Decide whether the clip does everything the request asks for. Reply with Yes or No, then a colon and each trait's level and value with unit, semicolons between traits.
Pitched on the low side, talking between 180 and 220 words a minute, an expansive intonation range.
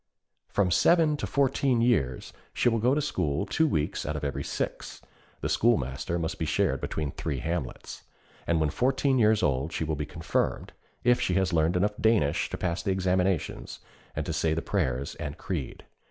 Yes: very low, 90 Hz; average, 185 wpm; wide, 7.0 semitones